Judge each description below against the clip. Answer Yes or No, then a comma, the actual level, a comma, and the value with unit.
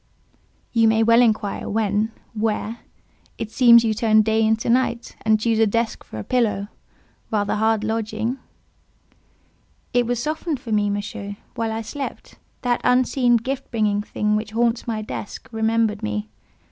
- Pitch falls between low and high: No, high, 220 Hz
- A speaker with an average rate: Yes, average, 150 wpm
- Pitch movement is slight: Yes, narrow, 1.7 semitones